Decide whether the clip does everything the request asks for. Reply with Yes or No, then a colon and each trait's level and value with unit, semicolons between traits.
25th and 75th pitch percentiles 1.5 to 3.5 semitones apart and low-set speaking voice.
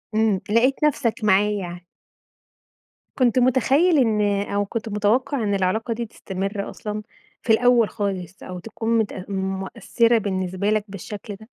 No: average, 3.1 semitones; high, 210 Hz